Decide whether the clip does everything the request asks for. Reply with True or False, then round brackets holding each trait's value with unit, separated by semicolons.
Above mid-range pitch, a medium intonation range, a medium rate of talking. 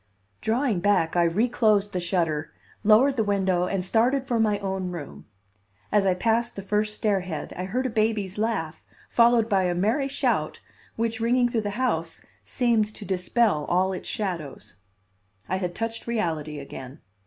True (205 Hz; 4.1 semitones; 165 wpm)